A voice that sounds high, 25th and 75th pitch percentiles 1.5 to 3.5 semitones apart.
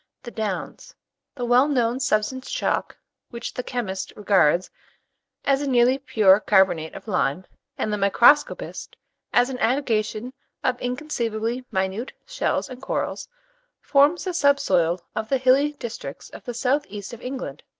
No: high, 240 Hz; average, 4.2 semitones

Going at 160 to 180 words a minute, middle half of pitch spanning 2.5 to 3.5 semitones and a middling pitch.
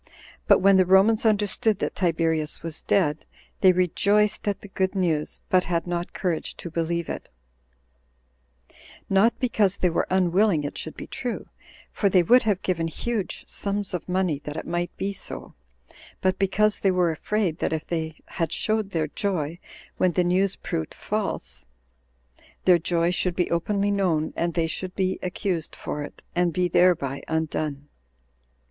Yes: average, 165 wpm; average, 3.2 semitones; medium, 180 Hz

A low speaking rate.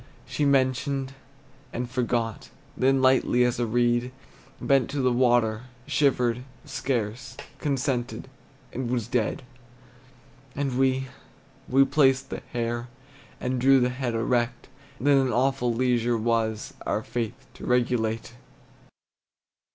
Yes: slow, 120 wpm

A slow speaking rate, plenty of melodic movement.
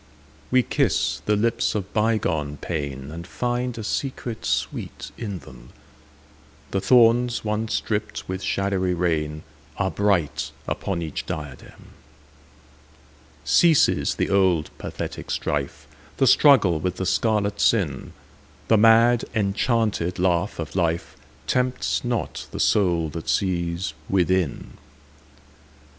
Yes: slow, 100 wpm; wide, 6.1 semitones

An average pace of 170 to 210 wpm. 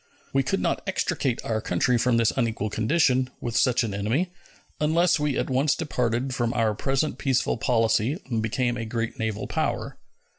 Yes: average, 175 wpm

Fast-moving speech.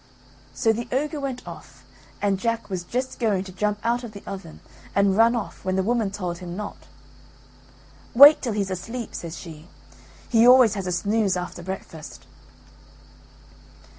No: average, 165 wpm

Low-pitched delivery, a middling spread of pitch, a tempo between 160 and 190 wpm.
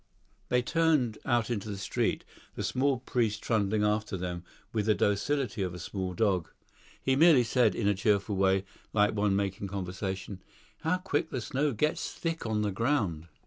Yes: low, 105 Hz; average, 4.4 semitones; average, 175 wpm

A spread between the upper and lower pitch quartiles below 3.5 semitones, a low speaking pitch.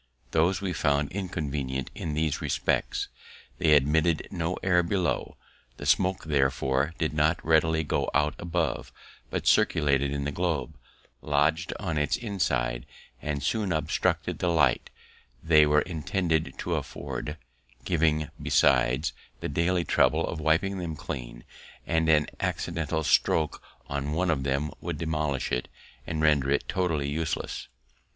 Yes: average, 2.7 semitones; very low, 80 Hz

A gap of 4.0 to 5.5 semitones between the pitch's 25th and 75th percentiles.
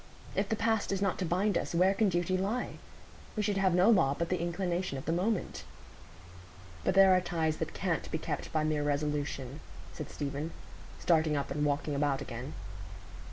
Yes: average, 4.4 semitones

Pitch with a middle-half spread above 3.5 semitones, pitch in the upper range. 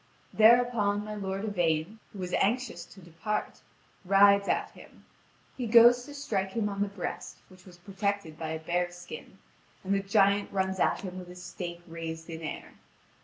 No: average, 2.8 semitones; high, 195 Hz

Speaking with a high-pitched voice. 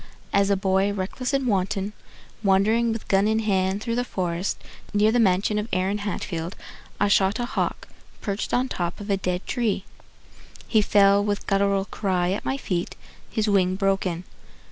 Yes: high, 200 Hz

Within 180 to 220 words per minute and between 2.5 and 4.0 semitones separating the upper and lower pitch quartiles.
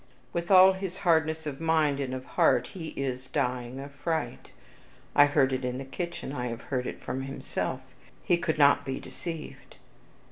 Yes: average, 185 wpm; average, 3.7 semitones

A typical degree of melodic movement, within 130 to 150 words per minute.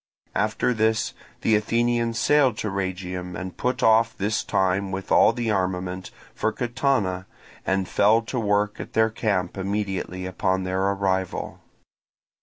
Yes: average, 3.1 semitones; average, 140 wpm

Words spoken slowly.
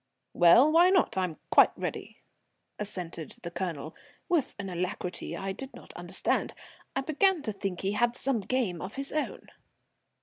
No: average, 160 wpm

